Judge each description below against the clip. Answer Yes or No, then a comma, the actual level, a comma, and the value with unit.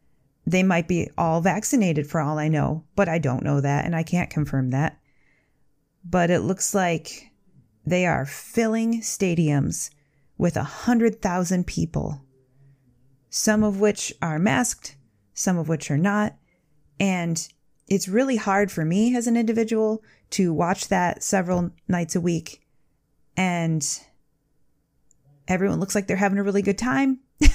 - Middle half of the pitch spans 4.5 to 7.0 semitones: Yes, average, 5.2 semitones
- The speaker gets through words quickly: No, average, 150 wpm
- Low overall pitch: No, medium, 170 Hz